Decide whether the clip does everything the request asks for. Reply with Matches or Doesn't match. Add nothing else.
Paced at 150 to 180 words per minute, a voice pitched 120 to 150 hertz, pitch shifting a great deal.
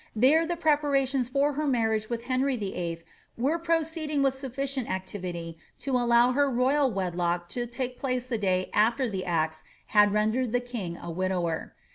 Doesn't match